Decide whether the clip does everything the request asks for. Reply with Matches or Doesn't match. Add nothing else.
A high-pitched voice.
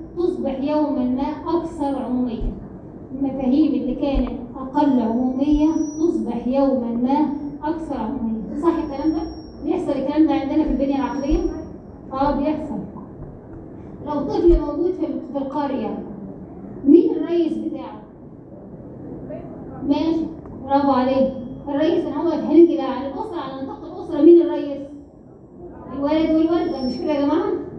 Matches